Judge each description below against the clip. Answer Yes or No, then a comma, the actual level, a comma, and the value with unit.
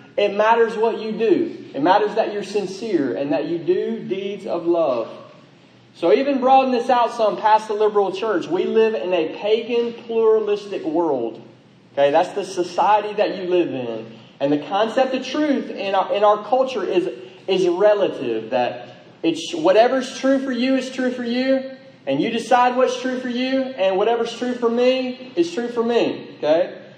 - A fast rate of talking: No, average, 180 wpm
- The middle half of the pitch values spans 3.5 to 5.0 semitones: Yes, average, 4.7 semitones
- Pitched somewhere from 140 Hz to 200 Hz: No, high, 230 Hz